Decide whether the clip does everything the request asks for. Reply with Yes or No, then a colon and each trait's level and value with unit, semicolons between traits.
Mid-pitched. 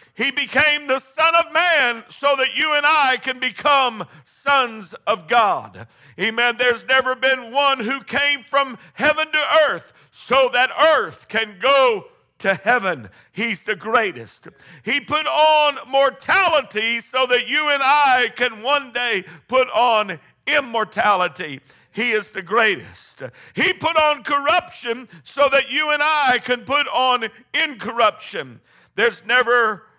No: very high, 255 Hz